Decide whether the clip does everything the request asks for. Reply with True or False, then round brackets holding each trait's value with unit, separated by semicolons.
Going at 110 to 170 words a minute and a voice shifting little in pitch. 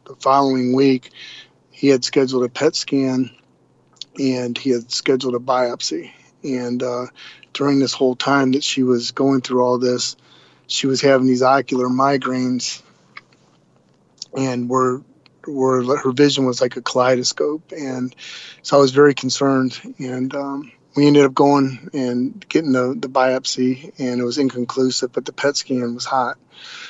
True (155 wpm; 1.6 semitones)